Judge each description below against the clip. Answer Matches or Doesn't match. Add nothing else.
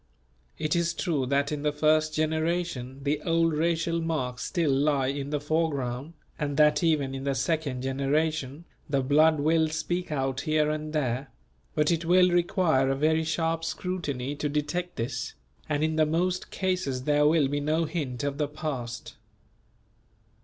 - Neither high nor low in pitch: Matches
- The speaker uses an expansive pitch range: Doesn't match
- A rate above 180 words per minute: Doesn't match